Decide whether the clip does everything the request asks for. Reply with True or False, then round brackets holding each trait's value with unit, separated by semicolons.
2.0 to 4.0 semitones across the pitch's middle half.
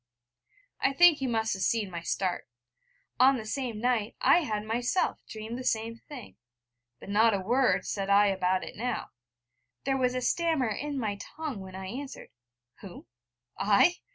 False (4.6 semitones)